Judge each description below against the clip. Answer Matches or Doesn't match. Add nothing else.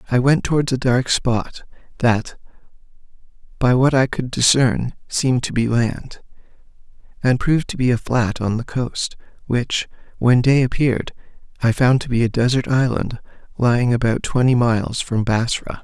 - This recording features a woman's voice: Doesn't match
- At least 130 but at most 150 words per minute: Doesn't match